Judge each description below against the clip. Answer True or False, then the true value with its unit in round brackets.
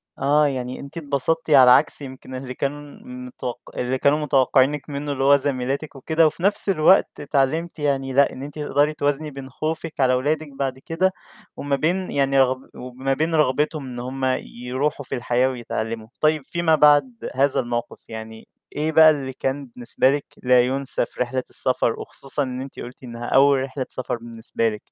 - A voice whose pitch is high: False (135 Hz)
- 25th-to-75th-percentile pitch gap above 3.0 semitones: False (2.7 semitones)